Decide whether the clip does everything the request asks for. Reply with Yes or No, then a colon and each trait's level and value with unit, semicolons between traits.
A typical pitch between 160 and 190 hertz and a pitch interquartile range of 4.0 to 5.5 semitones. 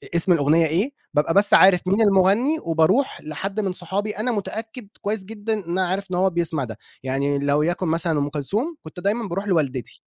Yes: medium, 185 Hz; average, 4.4 semitones